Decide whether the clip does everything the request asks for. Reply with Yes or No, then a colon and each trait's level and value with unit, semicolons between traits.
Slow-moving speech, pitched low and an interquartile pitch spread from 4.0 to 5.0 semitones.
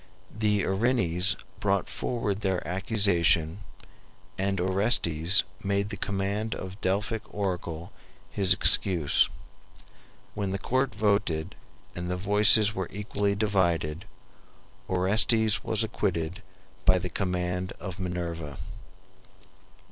No: slow, 105 wpm; very low, 95 Hz; narrow, 2.6 semitones